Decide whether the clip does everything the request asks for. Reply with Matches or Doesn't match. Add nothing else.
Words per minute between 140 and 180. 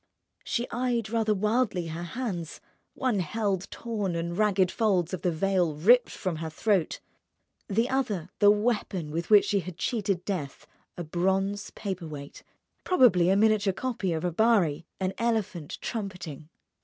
Matches